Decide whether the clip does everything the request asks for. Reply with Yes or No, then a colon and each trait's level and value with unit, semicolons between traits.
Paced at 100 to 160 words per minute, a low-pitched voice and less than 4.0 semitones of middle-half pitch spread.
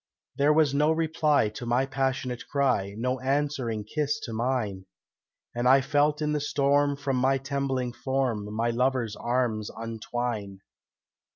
Yes: average, 145 wpm; low, 130 Hz; average, 3.4 semitones